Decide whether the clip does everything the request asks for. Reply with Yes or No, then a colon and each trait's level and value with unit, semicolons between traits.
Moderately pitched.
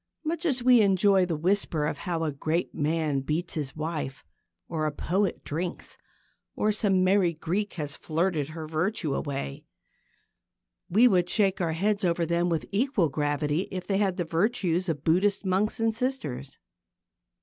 Yes: medium, 175 Hz